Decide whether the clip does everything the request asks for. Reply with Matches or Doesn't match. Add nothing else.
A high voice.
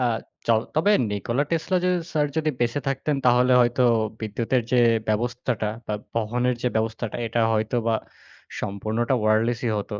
Doesn't match